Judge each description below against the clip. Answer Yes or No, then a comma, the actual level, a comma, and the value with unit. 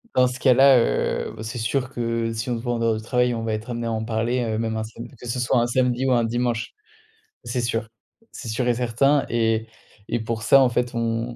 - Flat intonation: Yes, narrow, 1.5 semitones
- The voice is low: Yes, low, 120 Hz